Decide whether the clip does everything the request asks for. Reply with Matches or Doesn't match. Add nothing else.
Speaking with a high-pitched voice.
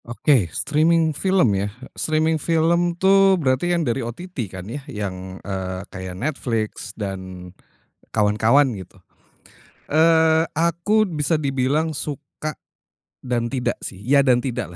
Doesn't match